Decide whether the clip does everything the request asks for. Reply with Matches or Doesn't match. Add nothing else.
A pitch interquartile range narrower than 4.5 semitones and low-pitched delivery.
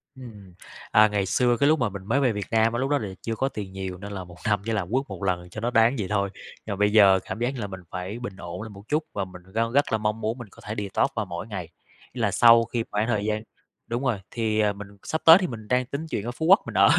Matches